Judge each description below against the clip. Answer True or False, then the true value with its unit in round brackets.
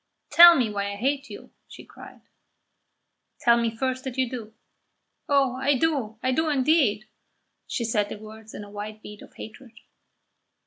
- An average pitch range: True (3.9 semitones)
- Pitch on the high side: True (240 Hz)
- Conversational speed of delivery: True (170 wpm)